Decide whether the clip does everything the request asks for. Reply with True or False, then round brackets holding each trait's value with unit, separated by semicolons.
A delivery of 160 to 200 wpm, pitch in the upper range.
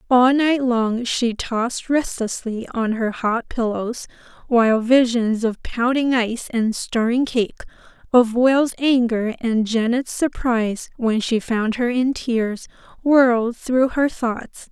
False (140 wpm; 240 Hz)